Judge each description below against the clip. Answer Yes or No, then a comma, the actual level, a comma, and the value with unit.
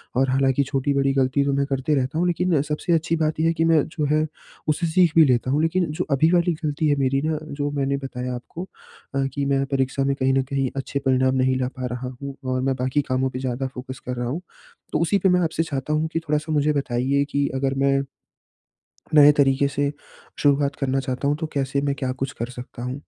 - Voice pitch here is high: No, medium, 140 Hz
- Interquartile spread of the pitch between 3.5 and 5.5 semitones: No, narrow, 2.5 semitones